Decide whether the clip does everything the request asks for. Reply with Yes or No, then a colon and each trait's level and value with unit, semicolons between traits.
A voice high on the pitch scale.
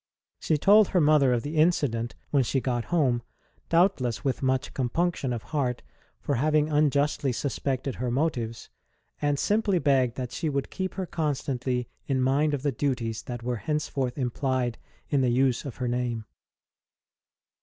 No: low, 135 Hz